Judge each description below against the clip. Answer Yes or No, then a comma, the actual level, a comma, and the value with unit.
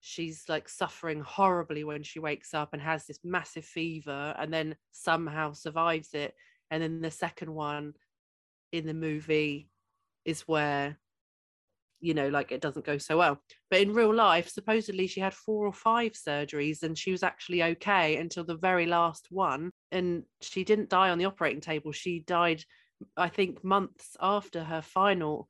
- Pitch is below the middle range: No, medium, 165 Hz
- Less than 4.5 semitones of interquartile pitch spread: Yes, average, 3.3 semitones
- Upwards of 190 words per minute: No, average, 170 wpm